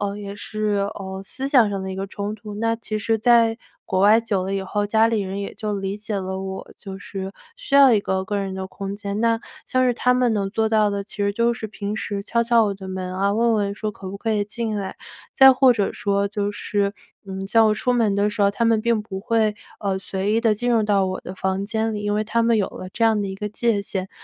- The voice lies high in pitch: Yes, high, 205 Hz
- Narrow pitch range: Yes, narrow, 2.3 semitones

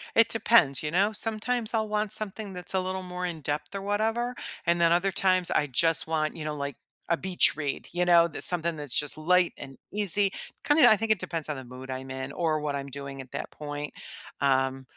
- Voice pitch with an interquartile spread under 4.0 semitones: No, wide, 5.5 semitones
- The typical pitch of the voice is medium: Yes, medium, 170 Hz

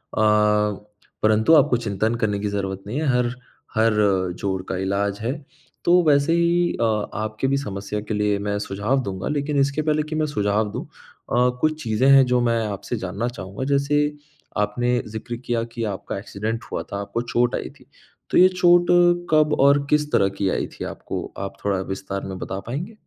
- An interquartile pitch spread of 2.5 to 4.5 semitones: No, wide, 5.5 semitones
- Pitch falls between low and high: No, low, 115 Hz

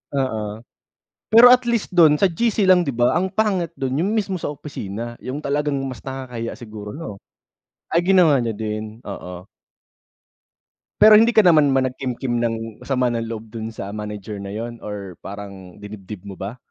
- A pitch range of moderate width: No, wide, 7.0 semitones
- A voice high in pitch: No, low, 120 Hz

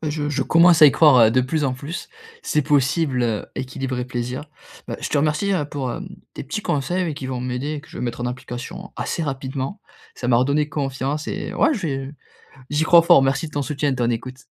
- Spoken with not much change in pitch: No, average, 3.1 semitones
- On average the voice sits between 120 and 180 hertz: Yes, medium, 140 Hz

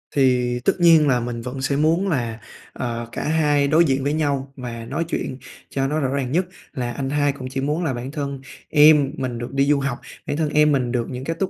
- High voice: No, medium, 140 Hz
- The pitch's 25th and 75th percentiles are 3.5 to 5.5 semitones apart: No, average, 3.0 semitones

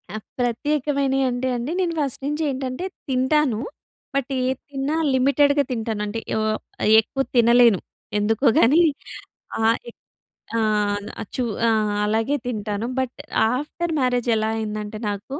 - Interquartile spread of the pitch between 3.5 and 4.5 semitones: Yes, average, 3.9 semitones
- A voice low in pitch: No, very high, 250 Hz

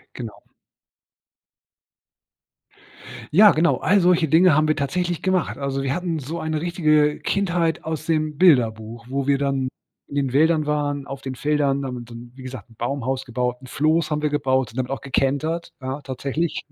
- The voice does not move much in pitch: No, average, 3.4 semitones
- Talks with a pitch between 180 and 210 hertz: No, medium, 145 Hz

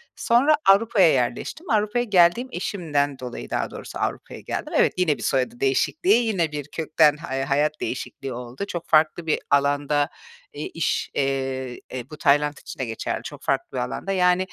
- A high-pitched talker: No, medium, 150 Hz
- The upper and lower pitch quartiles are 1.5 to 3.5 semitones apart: No, average, 5.2 semitones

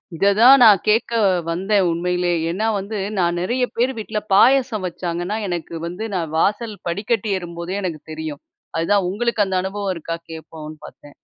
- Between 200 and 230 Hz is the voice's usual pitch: No, high, 190 Hz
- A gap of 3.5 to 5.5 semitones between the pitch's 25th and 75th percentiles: Yes, average, 3.9 semitones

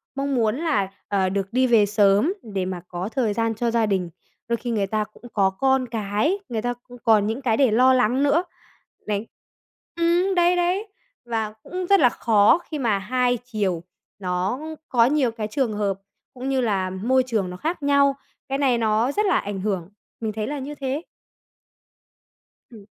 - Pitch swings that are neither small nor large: Yes, average, 4.7 semitones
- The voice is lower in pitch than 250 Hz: Yes, high, 230 Hz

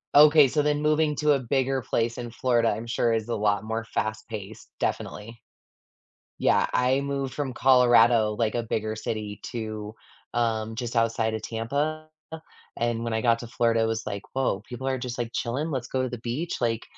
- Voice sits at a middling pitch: No, low, 120 Hz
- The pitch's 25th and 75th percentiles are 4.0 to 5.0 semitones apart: No, average, 2.8 semitones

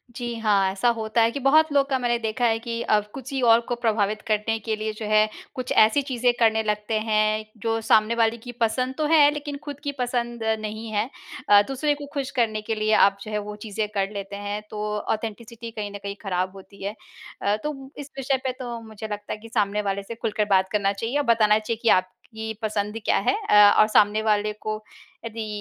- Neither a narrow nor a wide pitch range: No, narrow, 2.2 semitones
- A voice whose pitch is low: No, high, 220 Hz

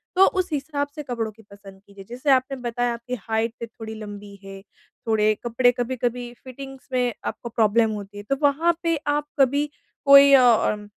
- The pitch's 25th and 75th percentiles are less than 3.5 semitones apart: No, average, 4.1 semitones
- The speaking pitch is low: No, high, 245 Hz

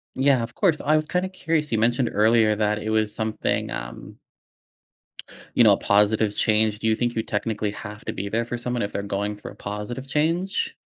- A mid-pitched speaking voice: No, low, 110 Hz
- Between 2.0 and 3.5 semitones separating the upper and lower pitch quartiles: No, average, 4.0 semitones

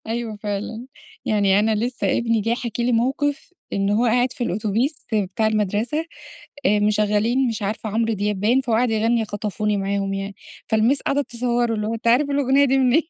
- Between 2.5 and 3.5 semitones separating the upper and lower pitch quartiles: Yes, average, 2.8 semitones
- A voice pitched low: No, high, 225 Hz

